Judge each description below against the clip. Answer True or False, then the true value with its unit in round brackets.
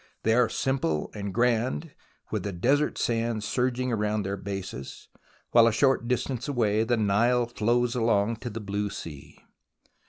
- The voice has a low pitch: True (115 Hz)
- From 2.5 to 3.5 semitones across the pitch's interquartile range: True (3.1 semitones)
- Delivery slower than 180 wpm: True (155 wpm)